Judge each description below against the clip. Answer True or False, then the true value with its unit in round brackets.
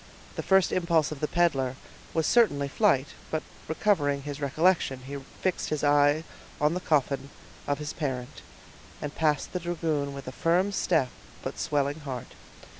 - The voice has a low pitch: False (150 Hz)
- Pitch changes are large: False (3.2 semitones)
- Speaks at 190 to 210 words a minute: False (160 wpm)